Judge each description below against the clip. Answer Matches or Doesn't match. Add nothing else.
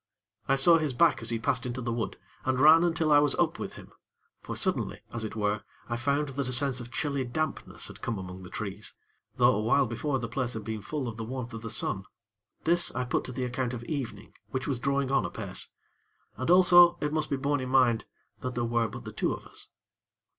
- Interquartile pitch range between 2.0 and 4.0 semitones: Matches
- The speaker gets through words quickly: Matches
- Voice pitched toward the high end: Doesn't match